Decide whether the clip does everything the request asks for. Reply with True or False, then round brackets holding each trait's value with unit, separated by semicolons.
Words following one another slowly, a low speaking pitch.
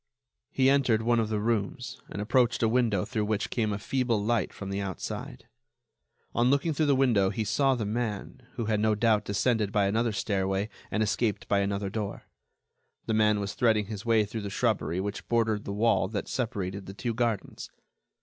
False (195 wpm; 110 Hz)